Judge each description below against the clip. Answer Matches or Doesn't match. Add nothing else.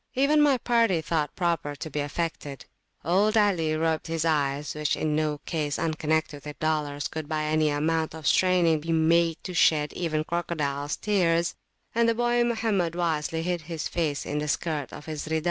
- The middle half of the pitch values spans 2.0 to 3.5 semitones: Matches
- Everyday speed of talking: Matches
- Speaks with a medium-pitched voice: Matches